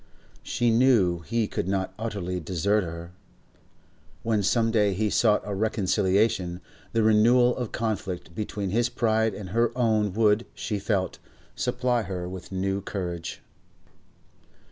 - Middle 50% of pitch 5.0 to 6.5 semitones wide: No, average, 3.4 semitones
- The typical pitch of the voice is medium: No, low, 105 Hz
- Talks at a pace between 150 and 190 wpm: No, slow, 135 wpm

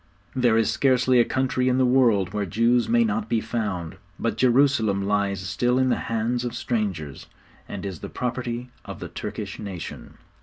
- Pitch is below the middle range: Yes, low, 115 Hz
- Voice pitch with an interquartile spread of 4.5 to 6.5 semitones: No, average, 3.6 semitones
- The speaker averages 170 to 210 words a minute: Yes, average, 180 wpm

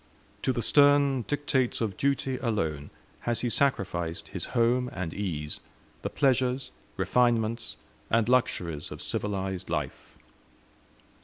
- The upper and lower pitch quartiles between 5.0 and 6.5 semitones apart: Yes, wide, 5.6 semitones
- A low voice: Yes, low, 115 Hz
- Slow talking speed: Yes, slow, 120 wpm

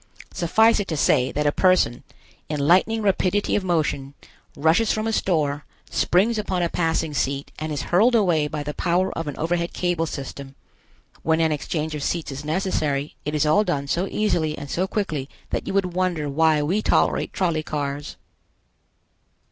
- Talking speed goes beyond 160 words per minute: Yes, average, 180 wpm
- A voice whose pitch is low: No, medium, 160 Hz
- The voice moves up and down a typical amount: Yes, average, 4.0 semitones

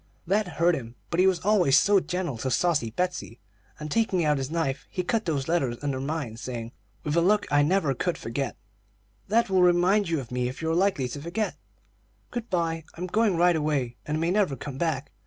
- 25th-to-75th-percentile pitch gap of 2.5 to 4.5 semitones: No, average, 5.0 semitones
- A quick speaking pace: Yes, fast, 210 wpm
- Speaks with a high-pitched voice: No, medium, 165 Hz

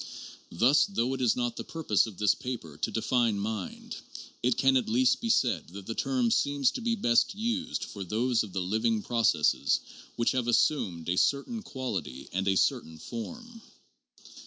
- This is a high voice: No, low, 120 Hz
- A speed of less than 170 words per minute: No, average, 180 wpm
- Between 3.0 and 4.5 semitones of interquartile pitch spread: No, average, 5.0 semitones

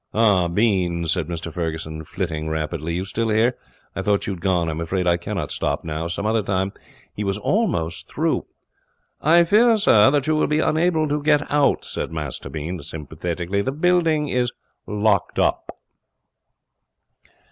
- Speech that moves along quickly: No, average, 170 wpm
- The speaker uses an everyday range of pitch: No, wide, 8.6 semitones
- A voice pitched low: Yes, very low, 95 Hz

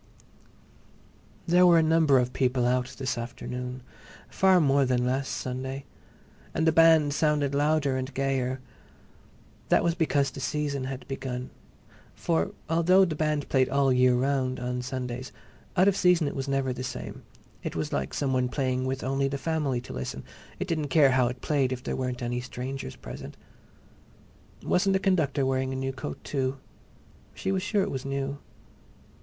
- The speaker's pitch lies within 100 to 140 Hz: Yes, low, 135 Hz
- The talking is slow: No, average, 175 wpm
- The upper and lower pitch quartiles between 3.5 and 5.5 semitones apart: No, average, 3.0 semitones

